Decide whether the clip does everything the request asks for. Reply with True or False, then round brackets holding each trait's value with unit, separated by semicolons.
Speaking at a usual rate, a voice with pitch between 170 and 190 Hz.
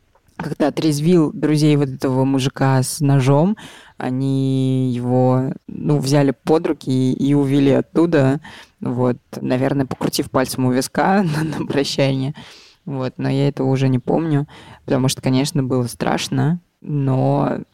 False (130 wpm; 140 Hz)